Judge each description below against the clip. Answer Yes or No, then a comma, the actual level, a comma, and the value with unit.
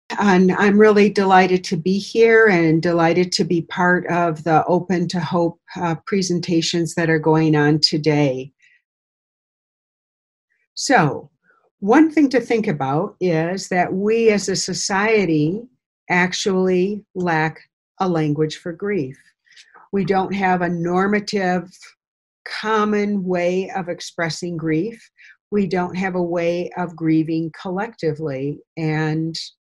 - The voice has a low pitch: No, medium, 180 Hz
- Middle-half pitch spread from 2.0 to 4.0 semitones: Yes, average, 3.3 semitones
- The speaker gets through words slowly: Yes, slow, 125 wpm